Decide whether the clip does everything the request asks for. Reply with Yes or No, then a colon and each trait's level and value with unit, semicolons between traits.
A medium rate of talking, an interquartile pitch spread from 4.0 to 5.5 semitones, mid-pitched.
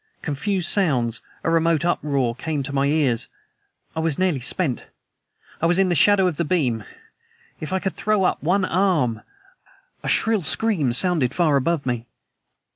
Yes: average, 165 wpm; average, 5.2 semitones; medium, 160 Hz